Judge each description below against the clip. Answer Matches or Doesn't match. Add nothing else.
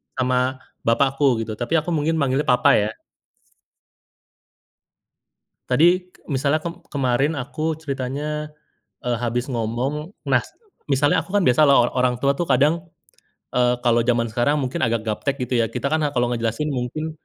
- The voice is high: Doesn't match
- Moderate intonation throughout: Matches